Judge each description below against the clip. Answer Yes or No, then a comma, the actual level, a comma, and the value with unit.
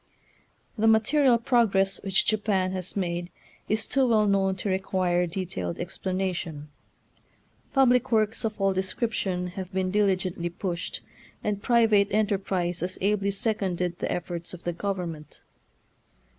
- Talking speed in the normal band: No, slow, 130 wpm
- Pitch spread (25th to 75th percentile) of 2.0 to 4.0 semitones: Yes, average, 3.0 semitones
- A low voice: No, high, 195 Hz